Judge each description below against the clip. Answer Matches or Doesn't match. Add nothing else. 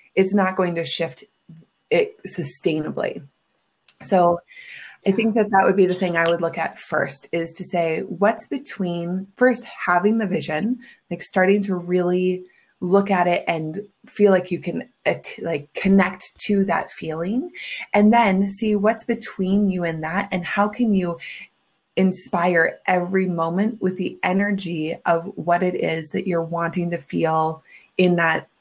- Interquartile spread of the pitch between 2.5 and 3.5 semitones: Matches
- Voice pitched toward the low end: Doesn't match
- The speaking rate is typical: Matches